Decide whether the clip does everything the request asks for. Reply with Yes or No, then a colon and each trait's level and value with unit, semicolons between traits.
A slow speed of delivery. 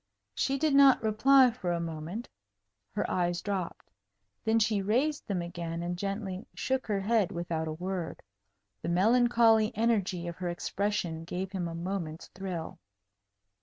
No: average, 150 wpm